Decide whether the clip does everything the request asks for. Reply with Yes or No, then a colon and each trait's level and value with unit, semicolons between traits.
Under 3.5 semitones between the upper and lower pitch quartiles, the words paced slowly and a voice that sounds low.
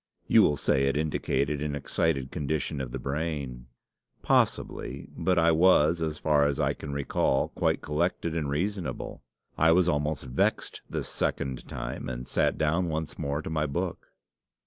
No: average, 2.7 semitones; average, 165 wpm; very low, 75 Hz